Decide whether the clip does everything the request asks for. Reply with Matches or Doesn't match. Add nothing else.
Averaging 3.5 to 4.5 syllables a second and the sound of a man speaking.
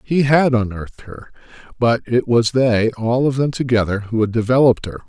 Doesn't match